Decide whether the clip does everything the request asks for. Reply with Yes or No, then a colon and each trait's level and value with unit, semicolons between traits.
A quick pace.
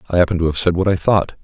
Yes: fast, 335 wpm